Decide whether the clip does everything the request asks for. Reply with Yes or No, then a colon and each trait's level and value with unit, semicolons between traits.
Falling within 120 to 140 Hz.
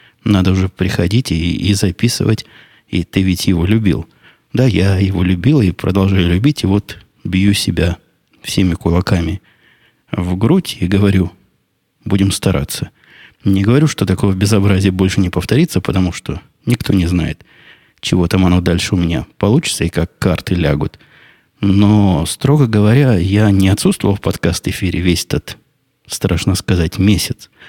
No: very low, 95 Hz